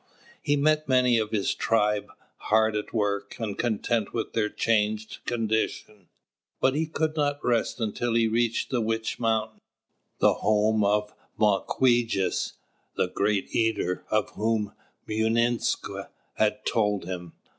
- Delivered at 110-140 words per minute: Yes, slow, 135 wpm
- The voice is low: Yes, low, 110 Hz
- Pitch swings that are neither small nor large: No, narrow, 2.1 semitones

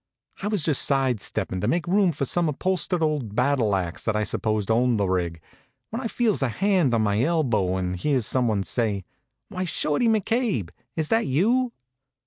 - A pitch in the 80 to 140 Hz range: Yes, low, 135 Hz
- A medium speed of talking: Yes, average, 190 wpm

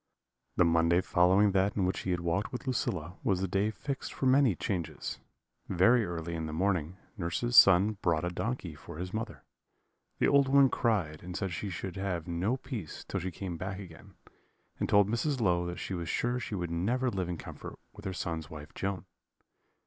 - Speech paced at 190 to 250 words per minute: Yes, average, 200 wpm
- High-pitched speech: No, very low, 95 Hz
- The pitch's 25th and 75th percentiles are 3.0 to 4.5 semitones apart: Yes, average, 3.9 semitones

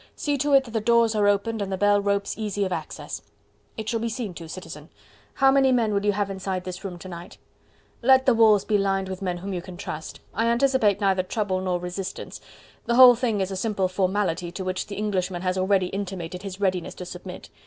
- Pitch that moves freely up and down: No, average, 3.1 semitones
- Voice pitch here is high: Yes, high, 195 Hz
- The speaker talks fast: Yes, fast, 230 wpm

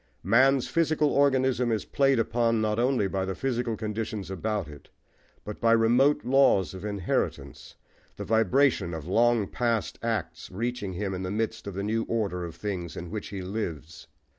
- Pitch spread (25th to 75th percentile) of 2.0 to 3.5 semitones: No, average, 4.0 semitones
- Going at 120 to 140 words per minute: No, average, 170 wpm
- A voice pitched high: No, low, 110 Hz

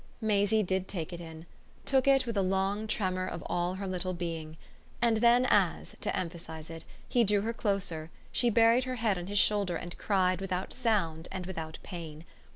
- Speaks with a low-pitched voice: No, high, 190 Hz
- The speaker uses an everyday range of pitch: Yes, average, 3.9 semitones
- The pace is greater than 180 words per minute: Yes, average, 190 wpm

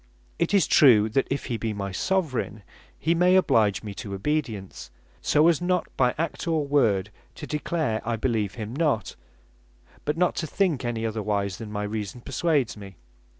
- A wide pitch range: Yes, wide, 6.6 semitones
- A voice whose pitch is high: No, low, 120 Hz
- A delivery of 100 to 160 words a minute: No, average, 175 wpm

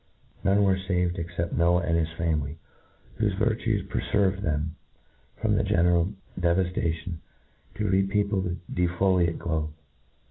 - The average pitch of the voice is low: Yes, very low, 90 Hz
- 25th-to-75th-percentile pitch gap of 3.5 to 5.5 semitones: No, average, 2.8 semitones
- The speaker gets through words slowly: Yes, slow, 130 wpm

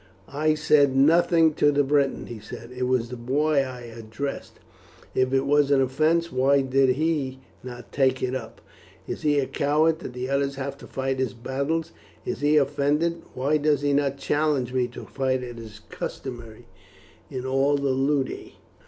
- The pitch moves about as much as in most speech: No, narrow, 2.3 semitones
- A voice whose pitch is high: No, low, 135 Hz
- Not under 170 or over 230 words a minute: Yes, average, 180 wpm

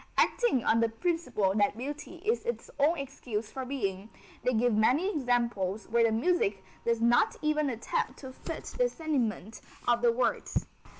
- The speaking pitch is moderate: No, high, 245 Hz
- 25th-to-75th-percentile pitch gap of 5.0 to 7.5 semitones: Yes, wide, 5.4 semitones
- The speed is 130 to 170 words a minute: Yes, average, 165 wpm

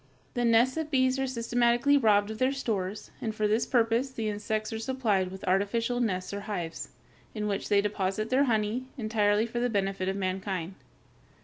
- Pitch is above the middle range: Yes, high, 220 Hz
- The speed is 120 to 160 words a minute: No, average, 185 wpm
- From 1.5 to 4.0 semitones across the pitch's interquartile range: Yes, average, 3.2 semitones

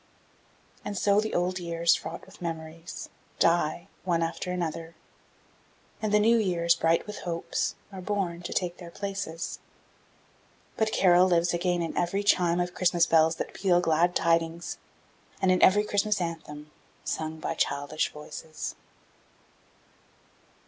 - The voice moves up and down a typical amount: No, narrow, 2.1 semitones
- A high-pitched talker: No, medium, 175 Hz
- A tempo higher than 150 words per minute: No, average, 140 wpm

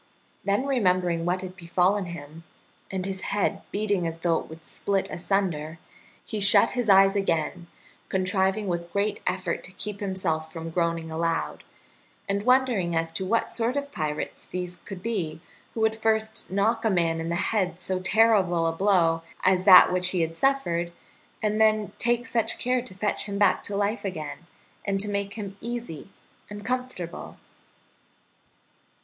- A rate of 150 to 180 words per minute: Yes, average, 165 wpm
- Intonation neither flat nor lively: Yes, average, 3.7 semitones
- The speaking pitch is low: No, high, 190 Hz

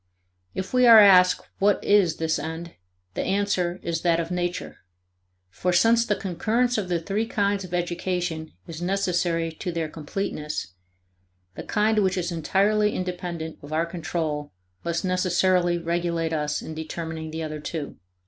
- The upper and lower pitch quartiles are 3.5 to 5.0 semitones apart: No, average, 3.0 semitones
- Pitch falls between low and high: Yes, medium, 175 Hz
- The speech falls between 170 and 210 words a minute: No, average, 155 wpm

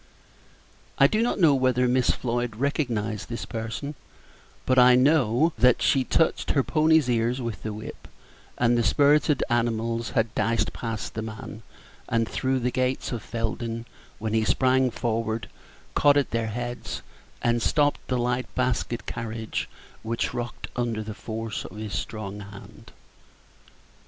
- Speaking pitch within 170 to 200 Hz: No, low, 120 Hz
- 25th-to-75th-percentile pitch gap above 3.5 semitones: No, narrow, 2.4 semitones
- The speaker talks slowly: No, average, 150 wpm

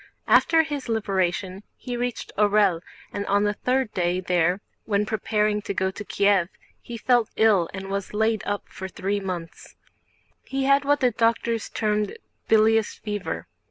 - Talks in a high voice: Yes, high, 210 Hz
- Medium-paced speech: Yes, average, 160 wpm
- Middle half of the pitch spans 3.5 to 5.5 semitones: No, average, 2.9 semitones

